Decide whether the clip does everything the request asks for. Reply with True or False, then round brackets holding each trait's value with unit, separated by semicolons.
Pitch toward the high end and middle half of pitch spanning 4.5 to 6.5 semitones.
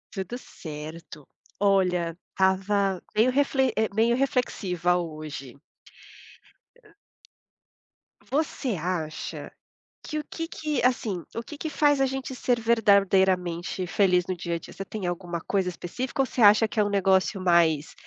True (195 Hz; 5.3 semitones)